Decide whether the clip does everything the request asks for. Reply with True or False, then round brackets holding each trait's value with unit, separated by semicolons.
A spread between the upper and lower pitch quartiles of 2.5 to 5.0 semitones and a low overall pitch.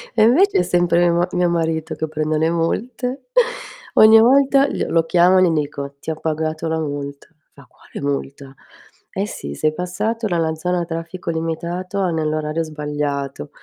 False (2.8 semitones; 165 Hz)